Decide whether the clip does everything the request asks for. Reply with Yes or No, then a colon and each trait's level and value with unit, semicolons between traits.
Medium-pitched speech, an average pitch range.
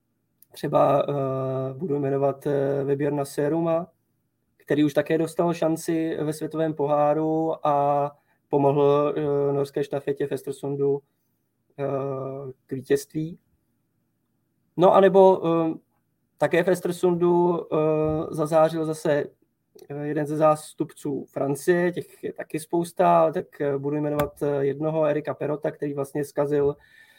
No: medium, 150 Hz; narrow, 2.3 semitones